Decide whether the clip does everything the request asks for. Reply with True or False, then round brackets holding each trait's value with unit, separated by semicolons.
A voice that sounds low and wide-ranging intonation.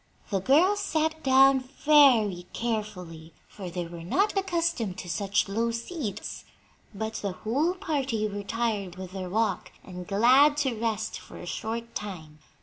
False (220 Hz; 6.0 semitones)